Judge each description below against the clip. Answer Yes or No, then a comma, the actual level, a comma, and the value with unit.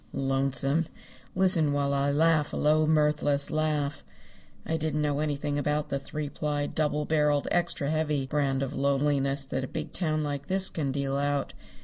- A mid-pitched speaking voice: Yes, medium, 145 Hz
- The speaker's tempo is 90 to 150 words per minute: No, average, 165 wpm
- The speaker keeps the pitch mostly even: Yes, narrow, 1.6 semitones